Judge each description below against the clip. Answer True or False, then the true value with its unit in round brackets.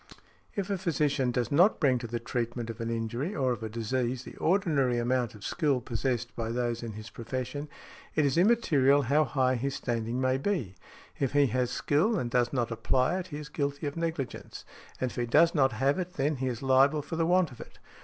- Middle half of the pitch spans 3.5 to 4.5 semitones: True (3.8 semitones)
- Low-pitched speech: True (130 Hz)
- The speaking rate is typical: False (220 wpm)